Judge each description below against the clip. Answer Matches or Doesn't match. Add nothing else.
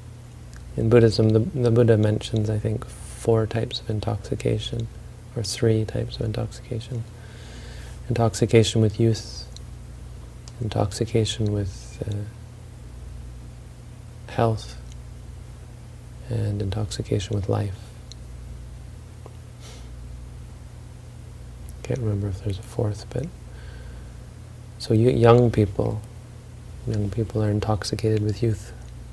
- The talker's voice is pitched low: Matches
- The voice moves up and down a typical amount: Doesn't match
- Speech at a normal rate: Doesn't match